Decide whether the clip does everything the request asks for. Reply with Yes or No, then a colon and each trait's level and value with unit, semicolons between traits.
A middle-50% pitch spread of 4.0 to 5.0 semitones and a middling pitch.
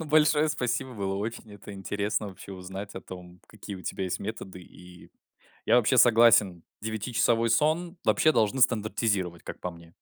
No: average, 4.3 semitones; low, 105 Hz